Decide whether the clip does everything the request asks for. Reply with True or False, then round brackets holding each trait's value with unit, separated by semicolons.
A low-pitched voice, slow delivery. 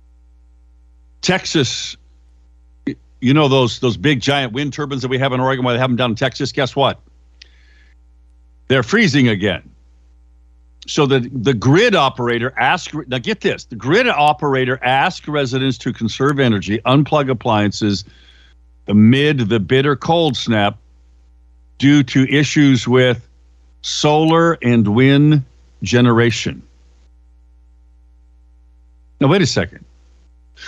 True (115 Hz; 120 wpm)